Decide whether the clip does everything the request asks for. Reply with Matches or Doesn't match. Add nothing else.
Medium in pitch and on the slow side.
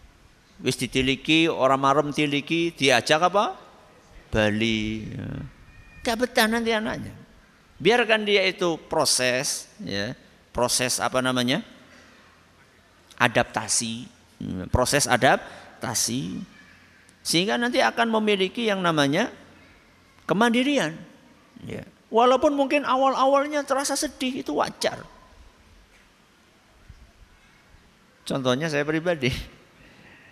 Matches